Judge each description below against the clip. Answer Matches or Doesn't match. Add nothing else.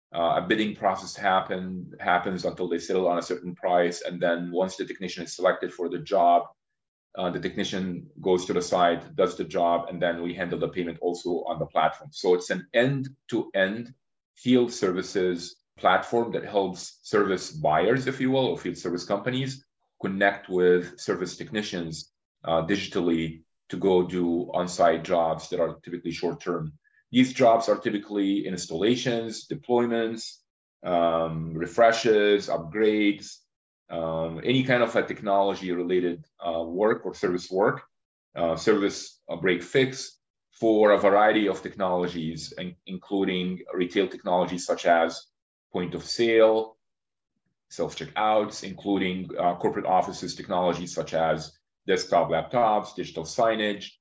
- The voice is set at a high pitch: Doesn't match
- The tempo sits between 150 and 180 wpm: Doesn't match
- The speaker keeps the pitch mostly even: Doesn't match